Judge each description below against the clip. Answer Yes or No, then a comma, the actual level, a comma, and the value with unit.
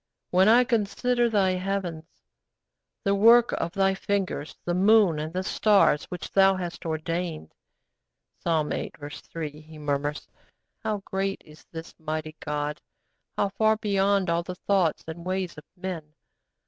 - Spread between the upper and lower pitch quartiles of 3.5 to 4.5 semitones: Yes, average, 4.0 semitones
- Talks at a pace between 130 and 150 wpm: Yes, average, 145 wpm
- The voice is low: No, medium, 180 Hz